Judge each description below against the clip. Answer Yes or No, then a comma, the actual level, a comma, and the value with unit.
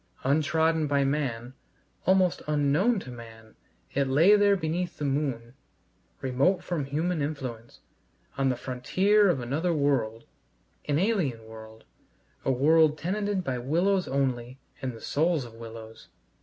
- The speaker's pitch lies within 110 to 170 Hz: Yes, medium, 140 Hz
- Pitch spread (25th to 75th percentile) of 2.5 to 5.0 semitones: No, wide, 5.6 semitones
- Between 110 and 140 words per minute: Yes, slow, 135 wpm